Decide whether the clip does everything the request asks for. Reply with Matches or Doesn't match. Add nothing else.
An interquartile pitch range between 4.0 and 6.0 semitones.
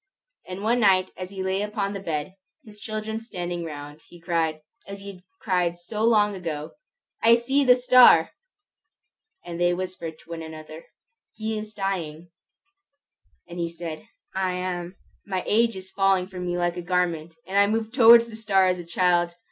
Doesn't match